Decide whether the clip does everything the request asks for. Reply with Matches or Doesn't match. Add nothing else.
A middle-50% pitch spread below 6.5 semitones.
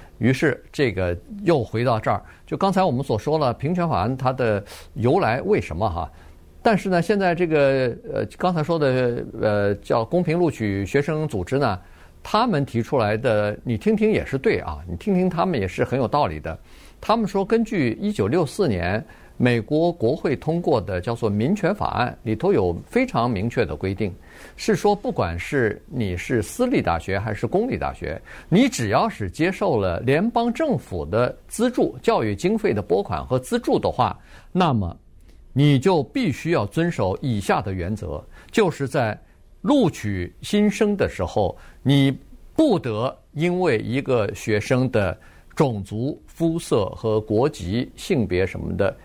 Doesn't match